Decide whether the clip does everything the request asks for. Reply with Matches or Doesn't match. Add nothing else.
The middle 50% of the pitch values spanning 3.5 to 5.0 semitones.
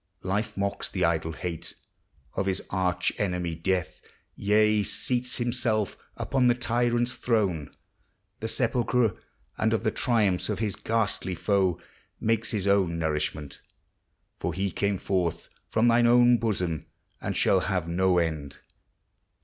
Matches